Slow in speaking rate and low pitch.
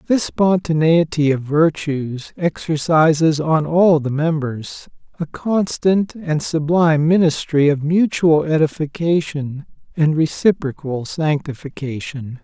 No: slow, 95 wpm; medium, 155 Hz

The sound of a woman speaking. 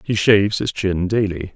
No: male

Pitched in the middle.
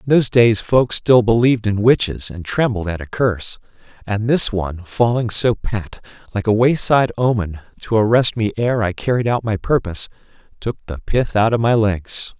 No: low, 110 Hz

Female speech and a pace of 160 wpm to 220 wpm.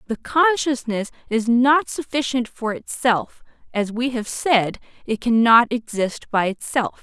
No: female; slow, 135 wpm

